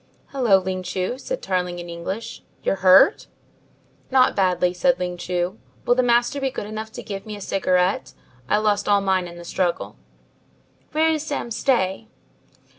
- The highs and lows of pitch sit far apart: No, average, 4.9 semitones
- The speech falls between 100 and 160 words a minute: No, average, 170 wpm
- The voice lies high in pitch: Yes, high, 195 Hz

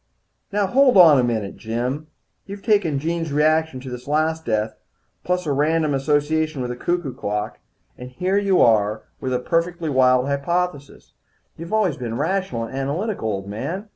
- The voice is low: No, medium, 150 Hz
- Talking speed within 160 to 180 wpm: Yes, average, 170 wpm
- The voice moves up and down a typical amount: No, wide, 5.7 semitones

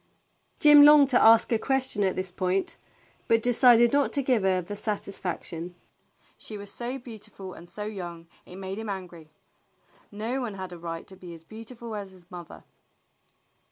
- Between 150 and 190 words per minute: Yes, average, 180 wpm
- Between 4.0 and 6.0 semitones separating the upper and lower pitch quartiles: Yes, average, 4.6 semitones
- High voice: Yes, high, 205 Hz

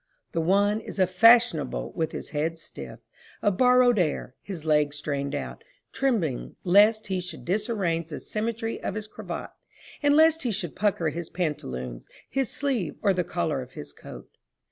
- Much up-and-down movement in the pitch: Yes, wide, 5.9 semitones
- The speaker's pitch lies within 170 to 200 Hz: Yes, medium, 185 Hz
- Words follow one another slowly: No, average, 165 wpm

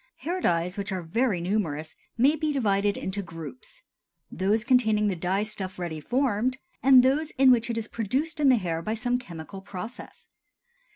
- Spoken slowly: No, average, 170 wpm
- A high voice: Yes, high, 210 Hz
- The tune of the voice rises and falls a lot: Yes, wide, 5.9 semitones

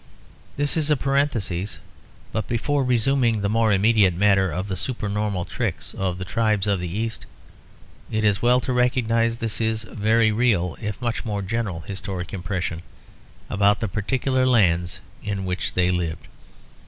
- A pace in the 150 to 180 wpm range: Yes, average, 155 wpm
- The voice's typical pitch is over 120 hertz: No, low, 105 Hz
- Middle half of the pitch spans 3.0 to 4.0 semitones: Yes, average, 3.6 semitones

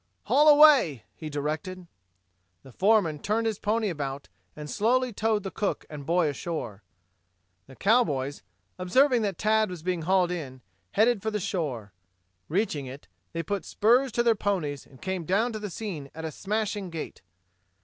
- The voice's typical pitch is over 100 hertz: Yes, medium, 185 Hz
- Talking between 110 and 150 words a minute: No, average, 160 wpm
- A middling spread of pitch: No, wide, 6.4 semitones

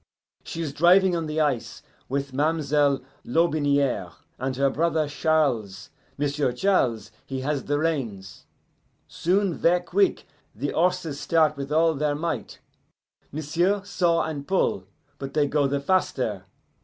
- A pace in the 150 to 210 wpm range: No, slow, 135 wpm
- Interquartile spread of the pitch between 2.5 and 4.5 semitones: Yes, average, 3.4 semitones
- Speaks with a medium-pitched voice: Yes, medium, 150 Hz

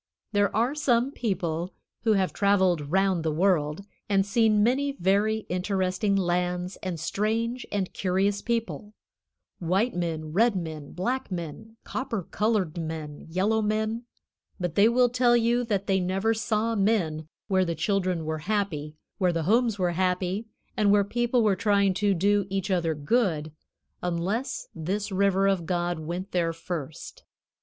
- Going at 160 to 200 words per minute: No, average, 150 wpm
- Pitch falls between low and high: No, high, 195 Hz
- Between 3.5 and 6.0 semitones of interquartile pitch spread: Yes, average, 3.9 semitones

